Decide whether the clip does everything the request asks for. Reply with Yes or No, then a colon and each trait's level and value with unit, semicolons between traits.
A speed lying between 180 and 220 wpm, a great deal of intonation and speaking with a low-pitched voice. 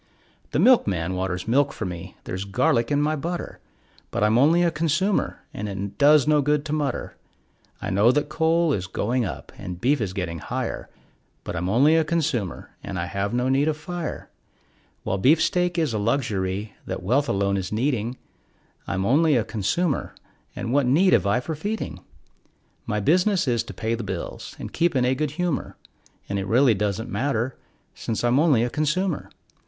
Yes: average, 185 wpm; wide, 7.2 semitones; low, 125 Hz